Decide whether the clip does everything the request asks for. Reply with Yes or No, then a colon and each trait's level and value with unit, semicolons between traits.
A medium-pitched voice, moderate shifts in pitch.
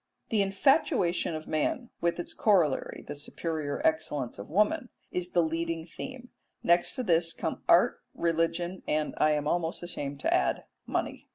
Yes: medium, 170 Hz; average, 3.3 semitones